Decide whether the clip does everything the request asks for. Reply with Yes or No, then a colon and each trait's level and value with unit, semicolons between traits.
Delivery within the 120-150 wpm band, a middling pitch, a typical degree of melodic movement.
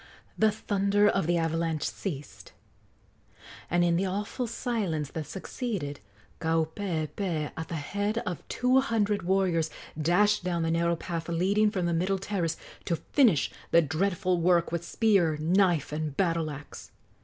Yes: average, 145 wpm; medium, 175 Hz; average, 3.7 semitones